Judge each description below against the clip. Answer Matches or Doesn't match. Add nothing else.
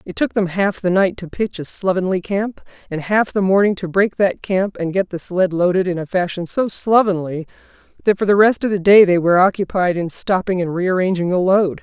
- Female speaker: Matches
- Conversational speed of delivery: Doesn't match